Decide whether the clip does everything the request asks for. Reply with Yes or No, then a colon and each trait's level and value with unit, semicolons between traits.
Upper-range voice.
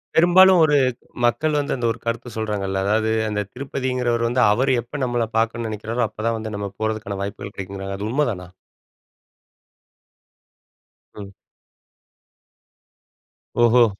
No: low, 115 Hz